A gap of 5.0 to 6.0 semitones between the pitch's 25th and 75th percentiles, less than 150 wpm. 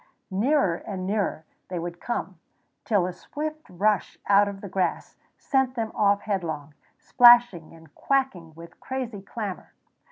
Yes: wide, 5.5 semitones; average, 140 wpm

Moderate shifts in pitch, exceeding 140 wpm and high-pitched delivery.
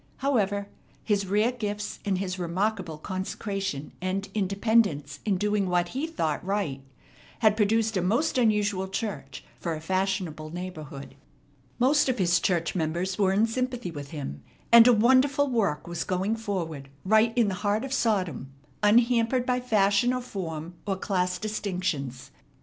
Yes: average, 4.2 semitones; average, 150 wpm; high, 200 Hz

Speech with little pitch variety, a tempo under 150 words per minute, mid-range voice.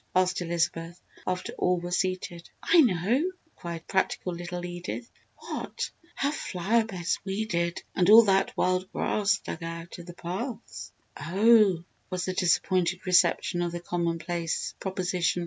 Yes: narrow, 2.1 semitones; average, 140 wpm; medium, 180 Hz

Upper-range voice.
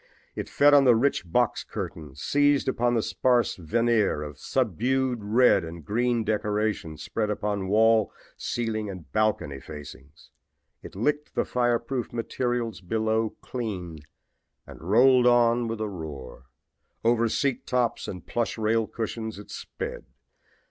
No: low, 110 Hz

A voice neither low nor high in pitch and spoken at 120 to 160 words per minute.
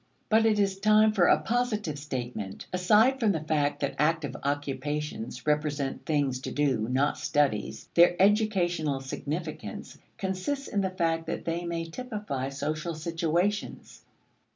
Yes: medium, 165 Hz; average, 140 wpm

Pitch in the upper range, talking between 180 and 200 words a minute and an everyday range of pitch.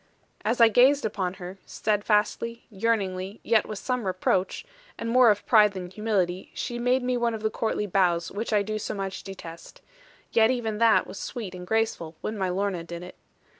Yes: high, 210 Hz; average, 190 wpm; average, 3.5 semitones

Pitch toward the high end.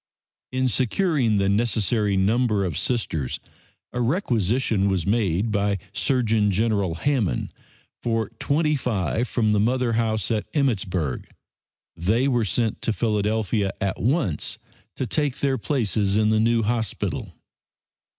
No: low, 110 Hz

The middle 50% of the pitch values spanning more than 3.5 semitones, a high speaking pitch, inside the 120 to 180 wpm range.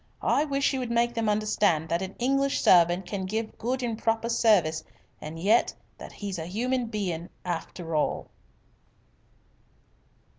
Yes: average, 5.1 semitones; high, 210 Hz; average, 155 wpm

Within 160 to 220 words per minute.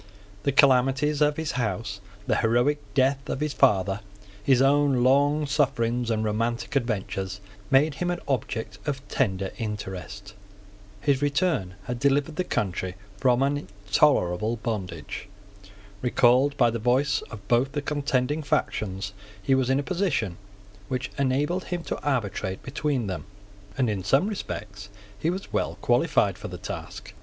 No: average, 150 wpm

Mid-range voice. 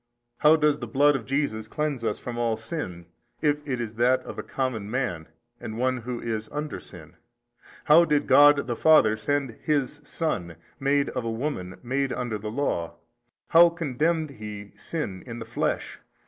No: low, 125 Hz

